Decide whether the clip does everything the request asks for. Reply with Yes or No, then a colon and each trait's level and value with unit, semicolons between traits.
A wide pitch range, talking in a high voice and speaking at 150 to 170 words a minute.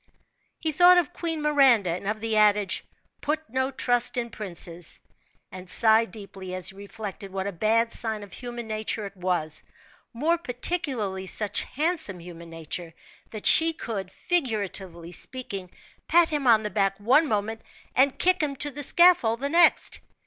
Yes: wide, 6.5 semitones; high, 220 Hz; average, 165 wpm